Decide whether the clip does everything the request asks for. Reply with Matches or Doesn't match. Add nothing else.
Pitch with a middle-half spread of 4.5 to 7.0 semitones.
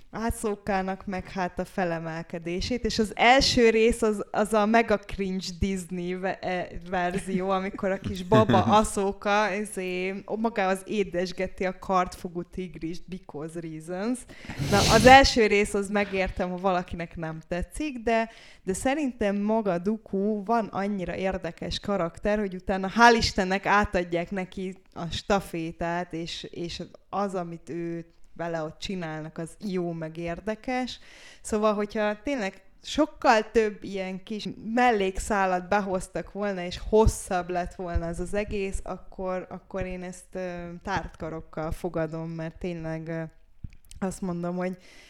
Doesn't match